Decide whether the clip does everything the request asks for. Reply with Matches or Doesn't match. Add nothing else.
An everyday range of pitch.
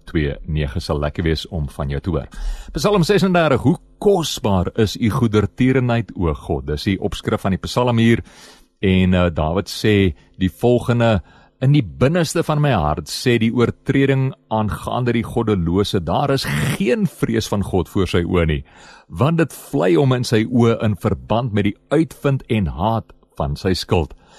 Doesn't match